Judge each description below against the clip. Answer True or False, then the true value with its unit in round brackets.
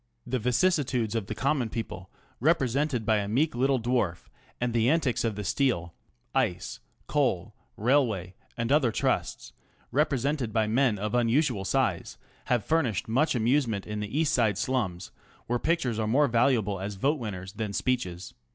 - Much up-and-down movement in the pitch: False (4.3 semitones)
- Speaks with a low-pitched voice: True (120 Hz)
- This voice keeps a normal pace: True (160 wpm)